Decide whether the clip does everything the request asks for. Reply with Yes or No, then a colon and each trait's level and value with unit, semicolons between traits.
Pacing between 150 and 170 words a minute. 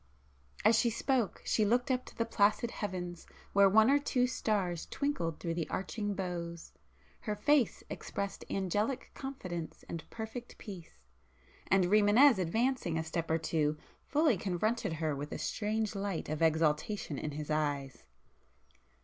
No: average, 140 wpm